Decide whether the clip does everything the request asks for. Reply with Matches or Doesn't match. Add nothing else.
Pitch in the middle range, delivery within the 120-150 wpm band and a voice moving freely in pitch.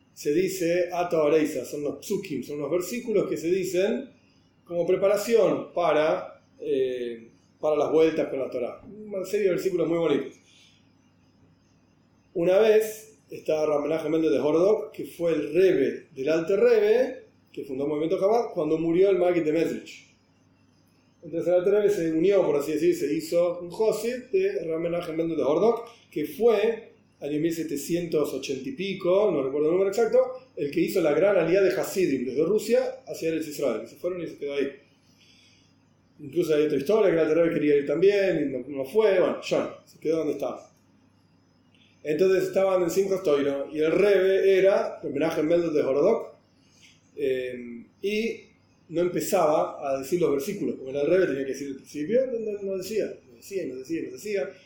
Doesn't match